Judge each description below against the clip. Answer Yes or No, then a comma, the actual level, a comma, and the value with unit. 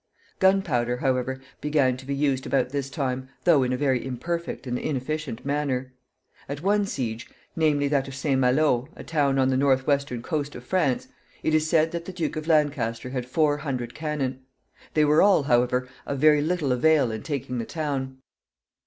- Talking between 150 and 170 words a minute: No, average, 180 wpm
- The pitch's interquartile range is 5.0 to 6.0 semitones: No, average, 3.3 semitones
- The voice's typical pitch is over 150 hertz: No, medium, 140 Hz